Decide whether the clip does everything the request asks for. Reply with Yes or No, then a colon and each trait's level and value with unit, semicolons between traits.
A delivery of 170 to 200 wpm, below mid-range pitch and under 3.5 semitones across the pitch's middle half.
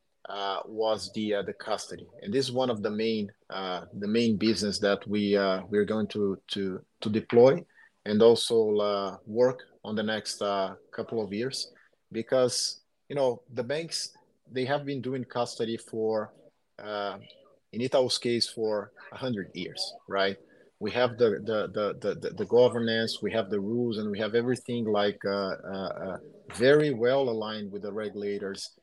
Yes: average, 175 wpm; low, 110 Hz; narrow, 2.6 semitones